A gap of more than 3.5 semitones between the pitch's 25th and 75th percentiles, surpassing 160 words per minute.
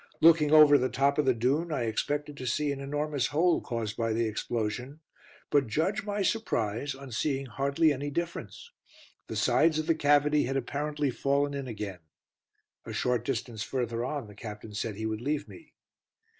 Yes: average, 4.2 semitones; average, 180 wpm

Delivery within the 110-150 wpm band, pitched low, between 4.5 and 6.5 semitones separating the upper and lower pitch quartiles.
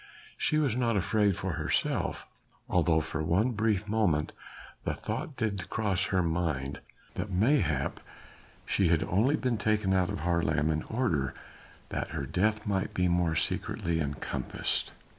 Yes: average, 145 wpm; very low, 95 Hz; average, 5.0 semitones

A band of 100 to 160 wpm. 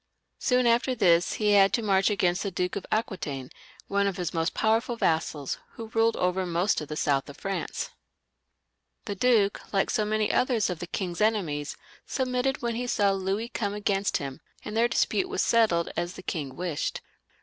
No: average, 185 wpm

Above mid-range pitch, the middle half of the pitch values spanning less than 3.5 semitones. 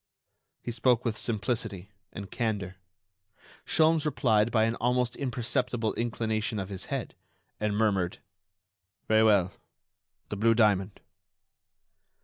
No: low, 110 Hz; average, 2.7 semitones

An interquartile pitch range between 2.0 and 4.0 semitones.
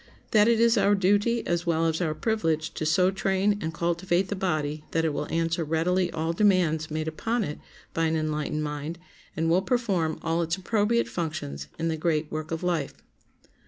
Yes: average, 3.5 semitones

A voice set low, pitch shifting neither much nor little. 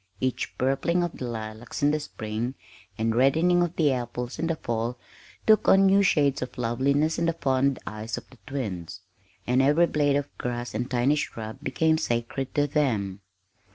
Yes: low, 130 Hz; average, 4.3 semitones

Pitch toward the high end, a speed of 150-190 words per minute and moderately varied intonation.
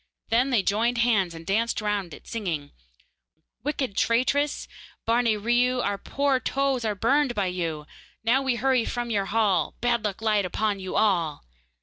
Yes: high, 225 Hz; average, 160 wpm; average, 3.8 semitones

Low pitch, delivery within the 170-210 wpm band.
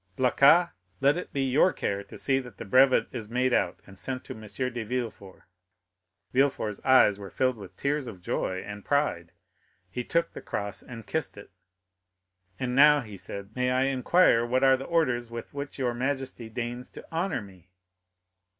Yes: low, 125 Hz; average, 180 wpm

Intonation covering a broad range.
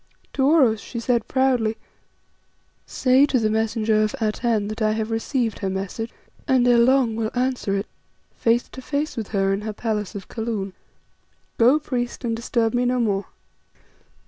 No: narrow, 2.6 semitones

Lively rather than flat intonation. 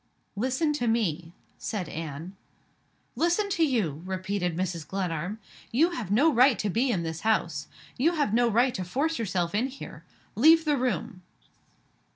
Yes: wide, 7.0 semitones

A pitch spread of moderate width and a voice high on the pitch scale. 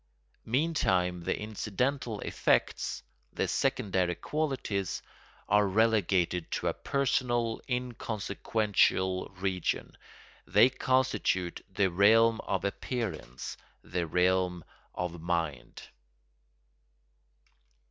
No: average, 4.8 semitones; low, 100 Hz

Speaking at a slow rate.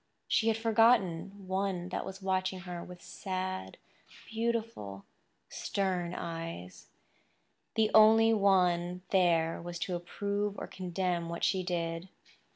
Yes: slow, 115 wpm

